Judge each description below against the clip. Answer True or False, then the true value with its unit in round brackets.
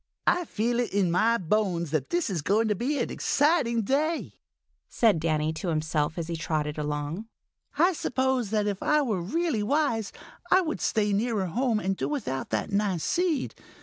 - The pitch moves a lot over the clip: True (7.6 semitones)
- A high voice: True (210 Hz)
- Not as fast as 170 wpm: False (180 wpm)